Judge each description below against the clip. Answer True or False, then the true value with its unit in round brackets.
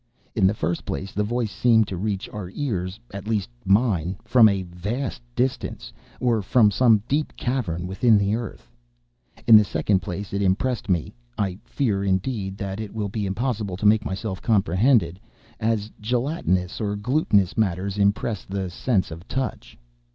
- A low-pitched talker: True (105 Hz)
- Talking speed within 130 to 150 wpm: False (160 wpm)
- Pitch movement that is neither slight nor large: True (3.4 semitones)